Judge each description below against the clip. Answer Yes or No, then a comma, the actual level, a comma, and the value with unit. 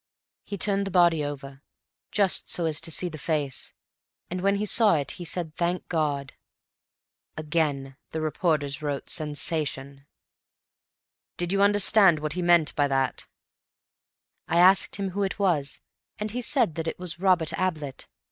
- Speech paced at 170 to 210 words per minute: No, average, 155 wpm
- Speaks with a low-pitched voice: No, medium, 165 Hz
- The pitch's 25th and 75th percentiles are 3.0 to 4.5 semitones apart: Yes, average, 4.2 semitones